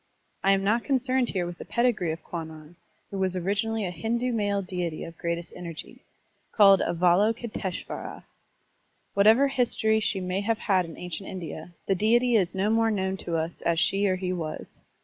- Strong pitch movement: No, average, 4.0 semitones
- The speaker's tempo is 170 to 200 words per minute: Yes, average, 180 wpm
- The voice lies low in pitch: No, high, 195 Hz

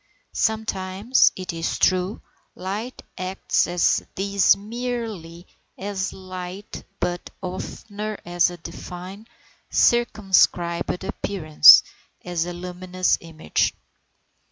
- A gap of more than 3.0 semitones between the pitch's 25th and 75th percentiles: No, narrow, 2.5 semitones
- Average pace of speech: No, slow, 90 wpm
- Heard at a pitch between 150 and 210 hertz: Yes, medium, 185 Hz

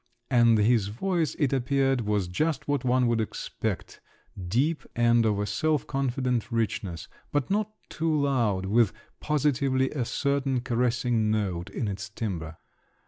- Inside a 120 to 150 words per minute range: Yes, average, 140 wpm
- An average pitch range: Yes, average, 4.7 semitones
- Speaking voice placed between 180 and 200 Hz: No, low, 120 Hz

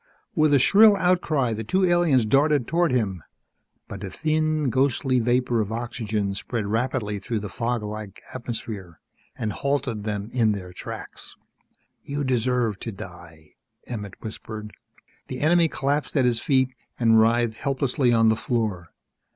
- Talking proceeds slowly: No, average, 150 wpm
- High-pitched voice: No, low, 120 Hz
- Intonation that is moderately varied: Yes, average, 4.4 semitones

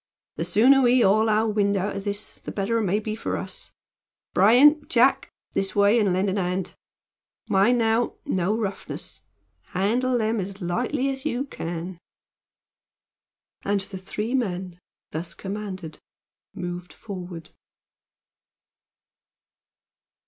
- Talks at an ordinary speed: No, slow, 125 wpm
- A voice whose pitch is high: Yes, high, 205 Hz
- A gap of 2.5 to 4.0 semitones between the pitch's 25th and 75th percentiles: Yes, average, 3.6 semitones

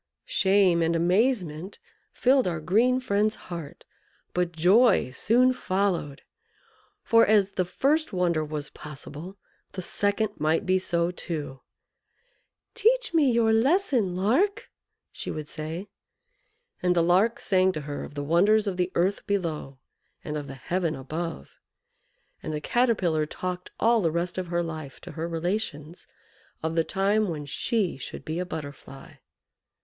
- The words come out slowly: No, average, 145 wpm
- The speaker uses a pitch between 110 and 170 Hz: No, medium, 180 Hz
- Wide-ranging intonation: No, average, 5.0 semitones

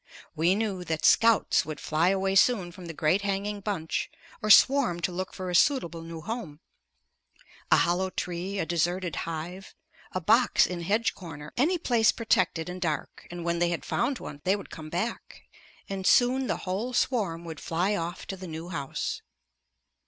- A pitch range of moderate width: Yes, average, 3.6 semitones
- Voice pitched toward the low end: No, medium, 185 Hz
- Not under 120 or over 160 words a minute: No, average, 180 wpm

